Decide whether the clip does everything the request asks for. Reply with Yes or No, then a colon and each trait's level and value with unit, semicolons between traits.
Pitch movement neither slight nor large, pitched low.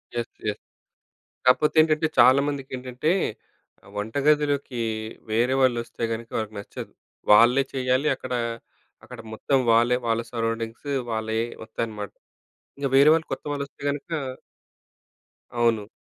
Yes: average, 3.7 semitones; low, 125 Hz